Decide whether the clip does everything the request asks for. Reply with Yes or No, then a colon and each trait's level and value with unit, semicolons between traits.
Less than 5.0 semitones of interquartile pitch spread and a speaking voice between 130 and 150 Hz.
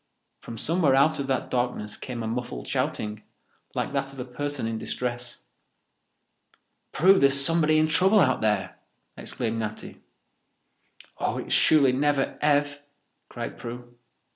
Yes: average, 3.6 semitones; low, 135 Hz